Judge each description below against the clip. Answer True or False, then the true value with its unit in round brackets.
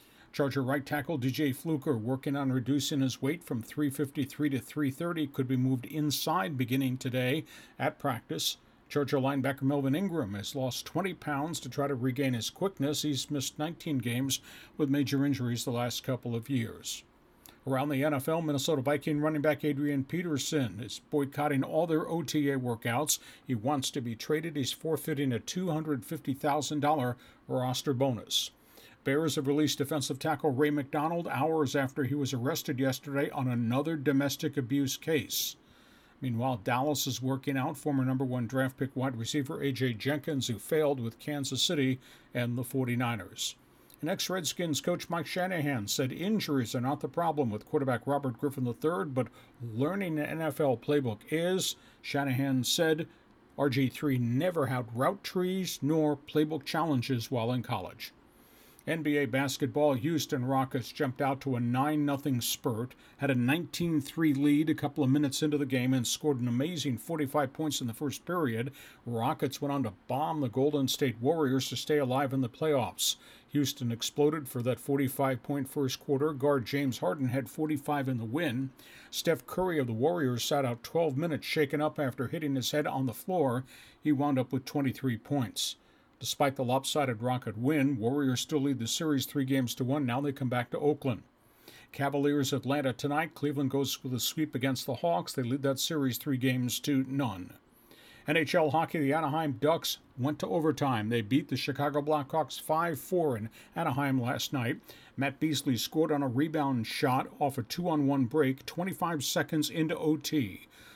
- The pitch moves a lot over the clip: False (2.6 semitones)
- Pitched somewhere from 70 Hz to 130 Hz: False (140 Hz)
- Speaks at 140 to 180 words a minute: True (170 wpm)